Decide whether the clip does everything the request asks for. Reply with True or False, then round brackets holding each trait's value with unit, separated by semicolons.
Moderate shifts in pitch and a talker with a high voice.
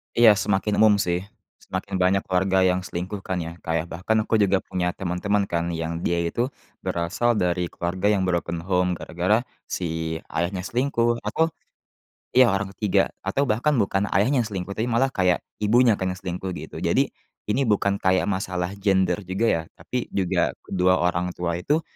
False (3.1 semitones; 95 Hz)